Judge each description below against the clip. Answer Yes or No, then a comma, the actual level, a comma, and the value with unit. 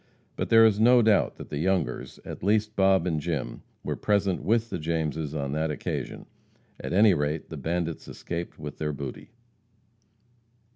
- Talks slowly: No, average, 165 wpm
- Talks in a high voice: No, very low, 85 Hz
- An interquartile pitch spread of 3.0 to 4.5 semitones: No, average, 5.1 semitones